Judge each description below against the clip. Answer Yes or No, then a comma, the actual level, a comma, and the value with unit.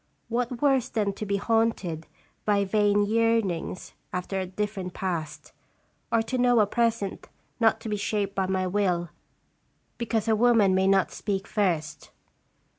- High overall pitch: Yes, high, 205 Hz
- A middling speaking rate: Yes, average, 150 wpm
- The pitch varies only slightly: No, average, 3.1 semitones